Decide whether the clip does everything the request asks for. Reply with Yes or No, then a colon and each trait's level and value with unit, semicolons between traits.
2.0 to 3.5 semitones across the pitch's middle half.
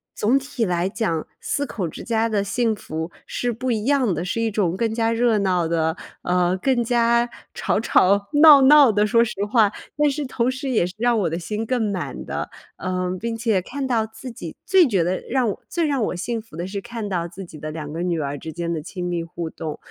No: average, 5.3 semitones